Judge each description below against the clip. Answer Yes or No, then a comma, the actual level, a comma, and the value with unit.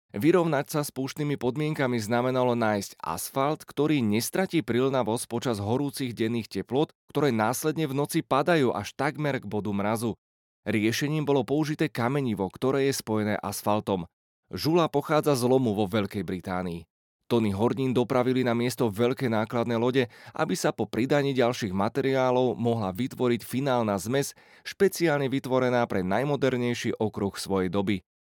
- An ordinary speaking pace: Yes, average, 140 wpm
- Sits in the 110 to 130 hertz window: Yes, low, 125 Hz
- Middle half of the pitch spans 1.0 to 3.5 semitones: No, average, 4.3 semitones